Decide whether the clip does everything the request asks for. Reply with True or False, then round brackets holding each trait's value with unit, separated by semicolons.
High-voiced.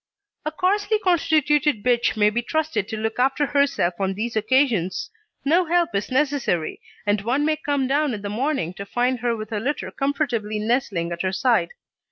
True (250 Hz)